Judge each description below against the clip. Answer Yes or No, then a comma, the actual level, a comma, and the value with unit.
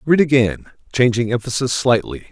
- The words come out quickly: No, slow, 130 wpm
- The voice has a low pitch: Yes, low, 120 Hz